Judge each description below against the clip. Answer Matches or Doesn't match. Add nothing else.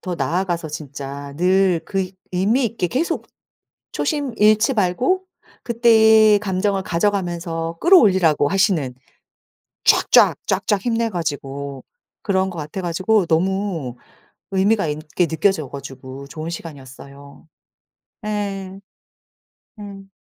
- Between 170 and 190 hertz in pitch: Matches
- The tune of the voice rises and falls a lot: Doesn't match